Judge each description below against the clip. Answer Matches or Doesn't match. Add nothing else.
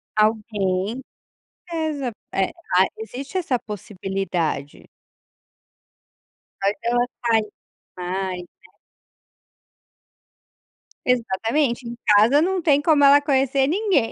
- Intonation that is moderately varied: Doesn't match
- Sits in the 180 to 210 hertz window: Doesn't match